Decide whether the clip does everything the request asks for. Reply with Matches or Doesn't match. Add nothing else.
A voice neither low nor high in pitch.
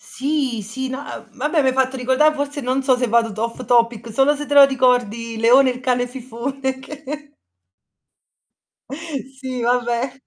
Doesn't match